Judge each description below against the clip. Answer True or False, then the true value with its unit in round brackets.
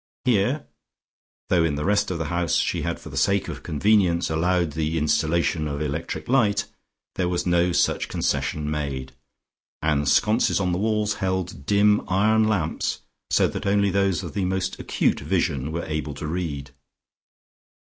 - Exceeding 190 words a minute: False (165 wpm)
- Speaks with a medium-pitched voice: False (90 Hz)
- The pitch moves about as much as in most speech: True (4.6 semitones)